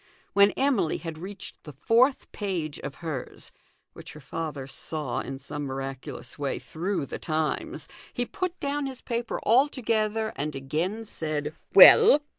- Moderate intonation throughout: No, wide, 7.6 semitones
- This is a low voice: No, medium, 165 Hz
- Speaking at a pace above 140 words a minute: Yes, average, 150 wpm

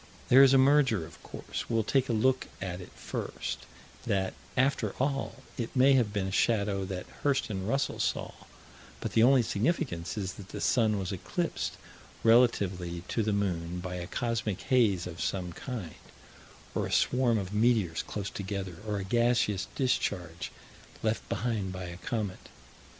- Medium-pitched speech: No, low, 105 Hz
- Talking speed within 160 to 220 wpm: Yes, average, 165 wpm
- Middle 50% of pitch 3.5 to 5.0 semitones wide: Yes, average, 4.7 semitones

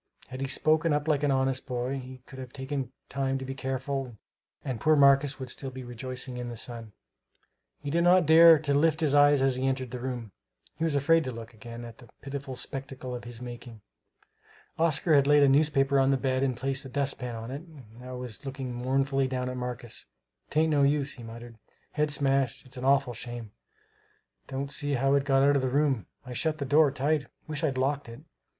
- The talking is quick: Yes, fast, 215 wpm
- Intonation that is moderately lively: No, narrow, 2.2 semitones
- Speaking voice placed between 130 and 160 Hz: Yes, low, 135 Hz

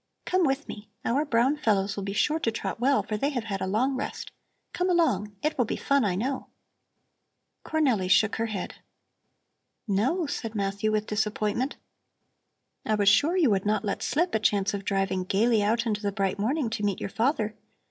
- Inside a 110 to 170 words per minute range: No, average, 195 wpm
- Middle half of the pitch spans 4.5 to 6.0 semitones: Yes, average, 5.0 semitones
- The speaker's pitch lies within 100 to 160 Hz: No, high, 220 Hz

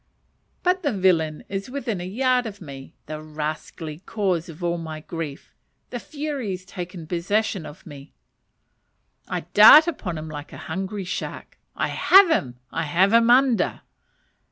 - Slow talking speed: No, average, 155 wpm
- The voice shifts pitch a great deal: Yes, wide, 6.6 semitones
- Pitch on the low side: No, medium, 180 Hz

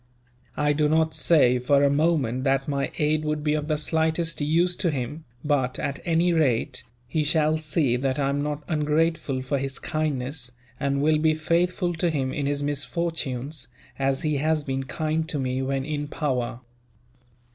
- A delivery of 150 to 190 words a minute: Yes, average, 180 wpm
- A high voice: No, medium, 150 Hz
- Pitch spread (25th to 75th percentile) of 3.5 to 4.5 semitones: No, narrow, 2.5 semitones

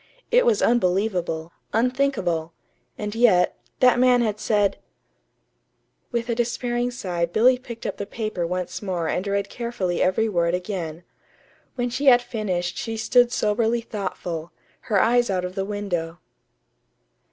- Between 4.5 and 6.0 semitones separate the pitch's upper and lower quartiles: Yes, average, 5.0 semitones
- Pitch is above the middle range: Yes, high, 210 Hz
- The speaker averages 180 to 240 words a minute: No, average, 140 wpm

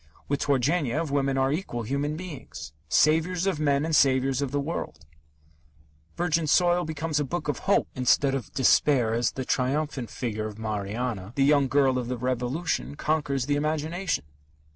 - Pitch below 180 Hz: Yes, medium, 140 Hz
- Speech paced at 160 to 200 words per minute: Yes, average, 165 wpm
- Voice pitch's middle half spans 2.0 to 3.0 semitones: No, average, 3.6 semitones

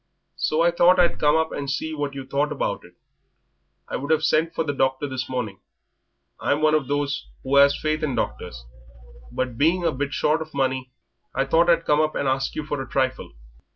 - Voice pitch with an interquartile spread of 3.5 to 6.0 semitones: No, average, 2.7 semitones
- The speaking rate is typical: No, fast, 215 wpm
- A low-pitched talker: No, medium, 145 Hz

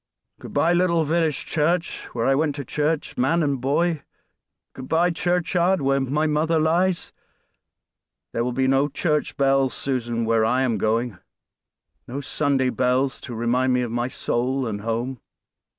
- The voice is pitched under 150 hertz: Yes, low, 135 Hz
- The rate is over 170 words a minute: No, average, 160 wpm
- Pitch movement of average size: Yes, average, 4.3 semitones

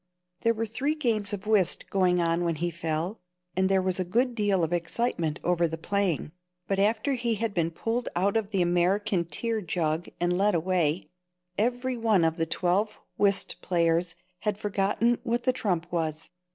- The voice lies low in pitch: No, high, 190 Hz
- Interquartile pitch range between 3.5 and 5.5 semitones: Yes, average, 4.3 semitones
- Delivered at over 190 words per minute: No, average, 180 wpm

